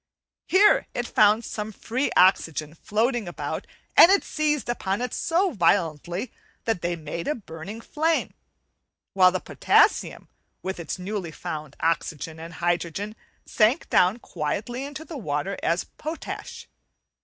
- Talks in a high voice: Yes, high, 205 Hz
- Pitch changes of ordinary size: No, wide, 6.7 semitones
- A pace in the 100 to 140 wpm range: Yes, slow, 135 wpm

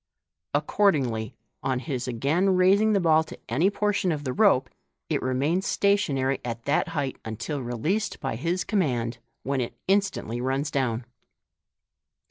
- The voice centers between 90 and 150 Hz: Yes, medium, 140 Hz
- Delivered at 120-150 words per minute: Yes, average, 140 wpm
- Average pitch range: No, wide, 6.6 semitones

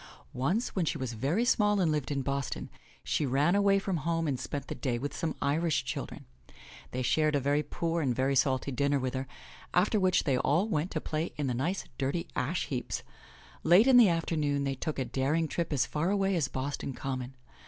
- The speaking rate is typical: No, fast, 210 wpm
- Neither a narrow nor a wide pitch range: Yes, average, 4.0 semitones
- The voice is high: No, medium, 150 Hz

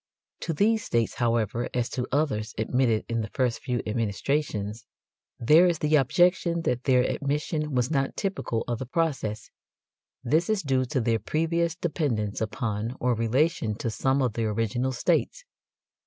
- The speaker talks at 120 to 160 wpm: Yes, average, 155 wpm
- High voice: No, low, 125 Hz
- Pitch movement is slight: No, average, 5.1 semitones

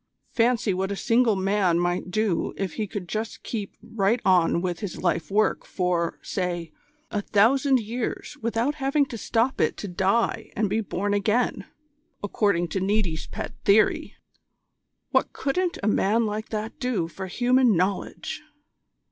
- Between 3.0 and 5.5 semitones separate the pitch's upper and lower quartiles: Yes, average, 3.6 semitones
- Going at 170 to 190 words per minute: No, average, 155 wpm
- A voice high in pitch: Yes, high, 205 Hz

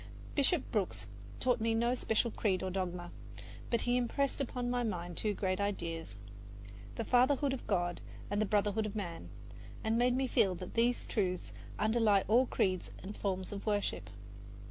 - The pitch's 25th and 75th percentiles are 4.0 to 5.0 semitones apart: Yes, average, 4.5 semitones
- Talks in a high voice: Yes, high, 210 Hz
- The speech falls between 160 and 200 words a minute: Yes, average, 165 wpm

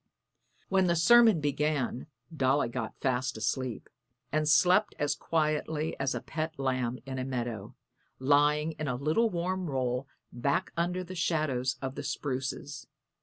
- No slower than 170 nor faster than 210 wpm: No, average, 145 wpm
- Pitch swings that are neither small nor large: Yes, average, 3.9 semitones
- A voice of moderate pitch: Yes, medium, 145 Hz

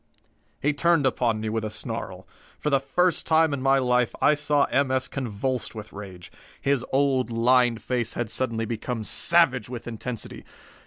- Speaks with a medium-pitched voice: No, low, 125 Hz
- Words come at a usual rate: Yes, average, 170 wpm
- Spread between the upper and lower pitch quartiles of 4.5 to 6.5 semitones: No, average, 3.5 semitones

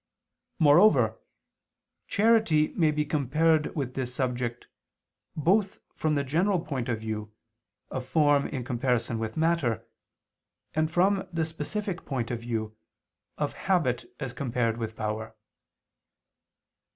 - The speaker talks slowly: Yes, slow, 120 wpm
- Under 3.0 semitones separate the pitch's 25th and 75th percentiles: No, wide, 5.4 semitones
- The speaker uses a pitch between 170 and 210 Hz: No, medium, 140 Hz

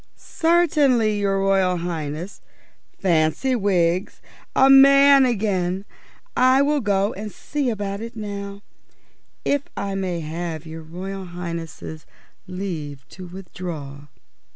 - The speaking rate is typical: No, slow, 110 wpm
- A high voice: Yes, high, 195 Hz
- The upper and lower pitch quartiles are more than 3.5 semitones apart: Yes, average, 4.7 semitones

